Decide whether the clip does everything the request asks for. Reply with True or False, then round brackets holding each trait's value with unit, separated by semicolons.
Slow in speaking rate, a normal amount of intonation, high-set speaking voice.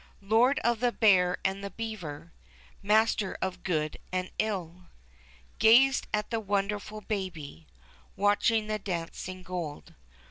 True (120 wpm; 3.3 semitones; 200 Hz)